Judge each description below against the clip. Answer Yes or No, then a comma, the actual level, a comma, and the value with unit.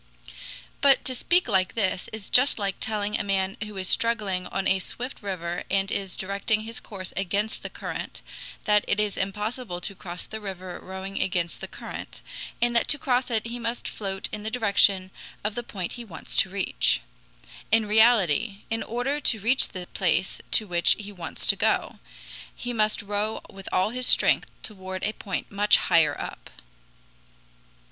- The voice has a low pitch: No, high, 205 Hz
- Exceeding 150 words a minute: Yes, average, 180 wpm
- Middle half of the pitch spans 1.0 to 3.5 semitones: Yes, average, 2.9 semitones